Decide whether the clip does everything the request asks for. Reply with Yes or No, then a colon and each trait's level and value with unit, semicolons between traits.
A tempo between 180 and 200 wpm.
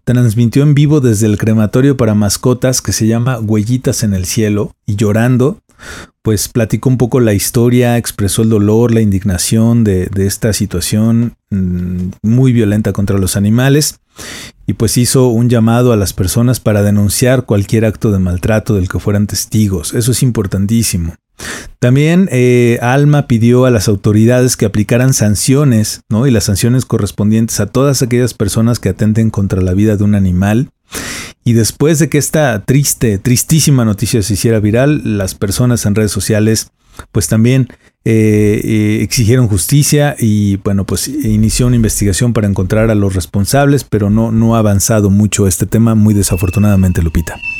No: average, 165 wpm